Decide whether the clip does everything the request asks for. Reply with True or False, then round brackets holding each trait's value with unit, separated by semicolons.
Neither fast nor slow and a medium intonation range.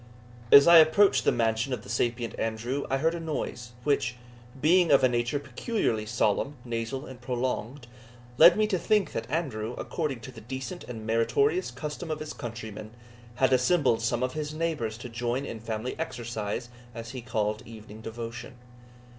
True (170 wpm; 4.5 semitones)